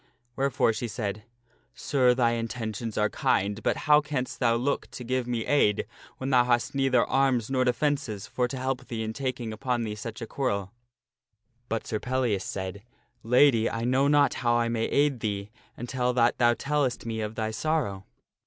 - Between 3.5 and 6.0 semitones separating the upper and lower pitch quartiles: No, average, 2.8 semitones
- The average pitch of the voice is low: Yes, low, 120 Hz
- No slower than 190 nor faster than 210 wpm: Yes, average, 195 wpm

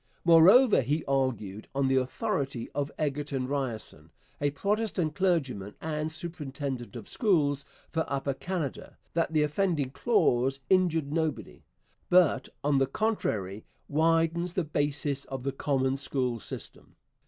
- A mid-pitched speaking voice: Yes, medium, 145 Hz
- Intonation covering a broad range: No, average, 3.7 semitones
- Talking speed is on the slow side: Yes, slow, 130 wpm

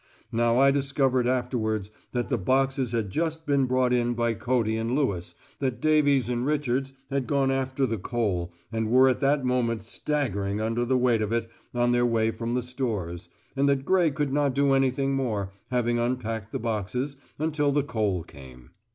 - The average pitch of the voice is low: Yes, low, 125 Hz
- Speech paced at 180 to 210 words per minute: Yes, average, 185 wpm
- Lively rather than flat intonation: No, average, 3.3 semitones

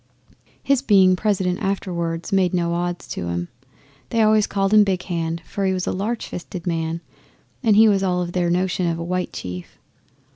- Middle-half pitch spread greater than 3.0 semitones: No, narrow, 2.6 semitones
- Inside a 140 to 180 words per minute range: No, average, 190 wpm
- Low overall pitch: No, medium, 180 Hz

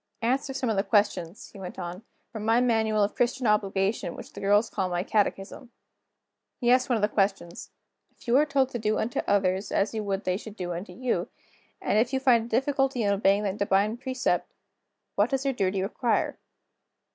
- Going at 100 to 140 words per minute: No, fast, 205 wpm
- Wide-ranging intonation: No, average, 3.9 semitones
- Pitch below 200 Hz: No, high, 215 Hz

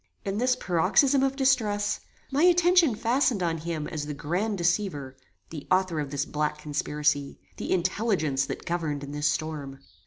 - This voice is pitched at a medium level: Yes, medium, 170 Hz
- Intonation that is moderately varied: No, wide, 6.8 semitones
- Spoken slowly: No, average, 160 wpm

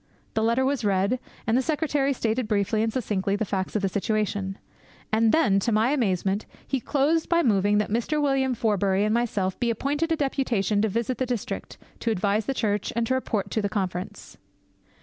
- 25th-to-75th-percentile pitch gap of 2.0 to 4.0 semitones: No, average, 4.4 semitones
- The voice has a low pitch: No, high, 220 Hz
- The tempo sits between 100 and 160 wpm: No, average, 190 wpm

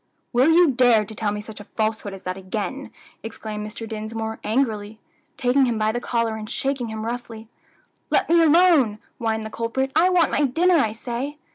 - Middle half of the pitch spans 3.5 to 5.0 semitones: Yes, average, 3.8 semitones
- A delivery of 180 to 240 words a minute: Yes, average, 195 wpm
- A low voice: No, high, 230 Hz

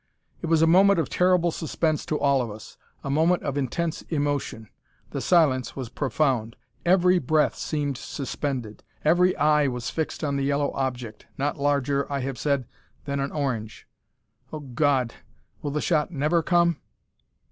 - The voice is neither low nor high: Yes, medium, 145 Hz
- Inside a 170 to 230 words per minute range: No, average, 160 wpm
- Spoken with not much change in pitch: No, average, 3.3 semitones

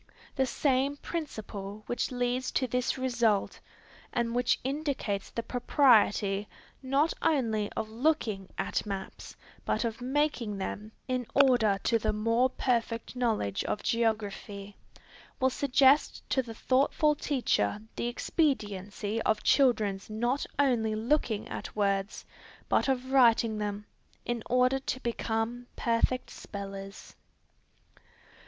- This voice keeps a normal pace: No, slow, 120 wpm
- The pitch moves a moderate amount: Yes, average, 3.6 semitones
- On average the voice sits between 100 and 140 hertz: No, high, 235 Hz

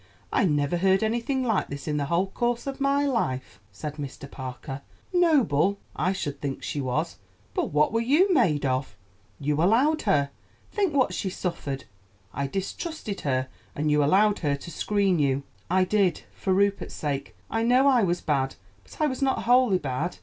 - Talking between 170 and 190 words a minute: Yes, average, 180 wpm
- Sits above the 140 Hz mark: Yes, medium, 185 Hz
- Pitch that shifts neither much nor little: No, wide, 8.8 semitones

